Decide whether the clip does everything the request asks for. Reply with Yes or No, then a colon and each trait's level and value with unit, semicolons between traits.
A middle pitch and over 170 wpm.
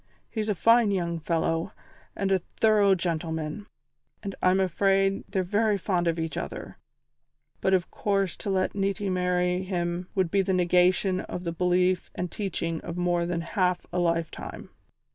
No: medium, 180 Hz; average, 160 wpm